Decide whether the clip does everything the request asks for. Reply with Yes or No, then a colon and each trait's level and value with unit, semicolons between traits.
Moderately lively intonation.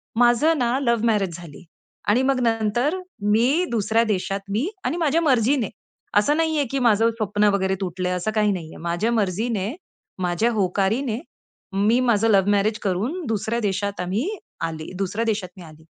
Yes: average, 3.8 semitones